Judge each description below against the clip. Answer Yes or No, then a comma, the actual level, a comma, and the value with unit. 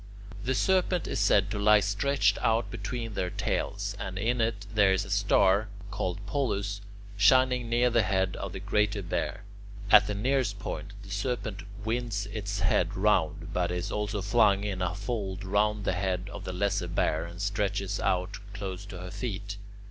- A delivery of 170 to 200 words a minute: Yes, average, 180 wpm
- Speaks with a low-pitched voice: Yes, low, 100 Hz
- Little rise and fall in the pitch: Yes, narrow, 2.1 semitones